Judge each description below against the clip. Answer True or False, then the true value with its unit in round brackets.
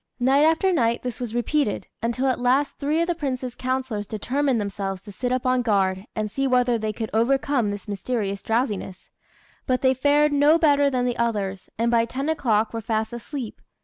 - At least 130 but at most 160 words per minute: False (195 wpm)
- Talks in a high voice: True (245 Hz)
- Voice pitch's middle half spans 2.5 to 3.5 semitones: False (4.0 semitones)